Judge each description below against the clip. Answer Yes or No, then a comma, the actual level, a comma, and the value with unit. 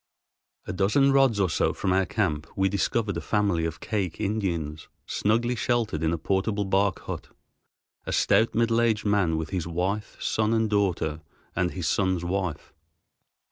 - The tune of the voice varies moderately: Yes, average, 3.8 semitones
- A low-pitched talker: Yes, low, 100 Hz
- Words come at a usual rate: Yes, average, 165 wpm